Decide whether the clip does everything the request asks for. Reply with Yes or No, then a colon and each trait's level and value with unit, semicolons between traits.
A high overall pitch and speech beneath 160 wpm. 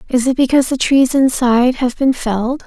No: very high, 255 Hz; average, 200 wpm